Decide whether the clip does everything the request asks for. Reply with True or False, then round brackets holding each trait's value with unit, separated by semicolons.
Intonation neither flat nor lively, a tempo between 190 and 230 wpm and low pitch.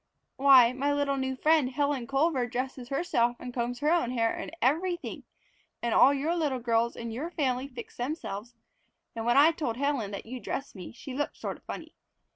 False (3.1 semitones; 195 wpm; 260 Hz)